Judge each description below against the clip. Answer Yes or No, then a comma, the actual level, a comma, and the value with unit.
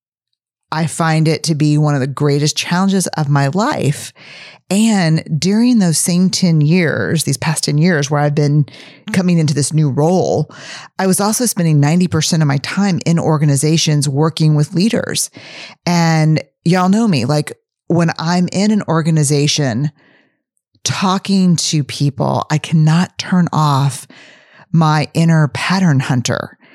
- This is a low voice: No, medium, 160 Hz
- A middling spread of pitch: Yes, average, 3.4 semitones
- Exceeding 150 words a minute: No, average, 145 wpm